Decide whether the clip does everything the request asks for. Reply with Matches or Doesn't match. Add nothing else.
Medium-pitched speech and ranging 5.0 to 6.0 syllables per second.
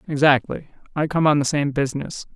Matches